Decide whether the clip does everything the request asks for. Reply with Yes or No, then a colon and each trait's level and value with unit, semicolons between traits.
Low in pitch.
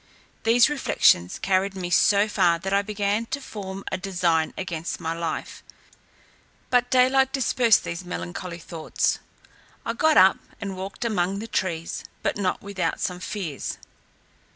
No: high, 195 Hz